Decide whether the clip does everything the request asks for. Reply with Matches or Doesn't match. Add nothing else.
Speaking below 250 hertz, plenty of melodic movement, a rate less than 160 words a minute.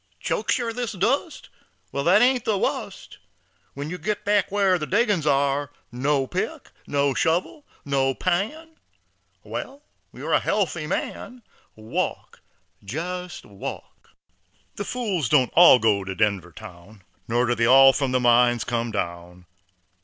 Matches